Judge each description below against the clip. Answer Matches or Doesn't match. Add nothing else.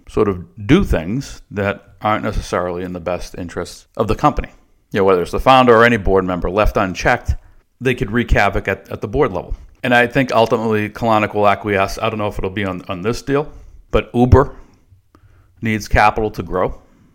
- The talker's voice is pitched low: Matches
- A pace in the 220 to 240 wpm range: Doesn't match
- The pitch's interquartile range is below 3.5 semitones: Doesn't match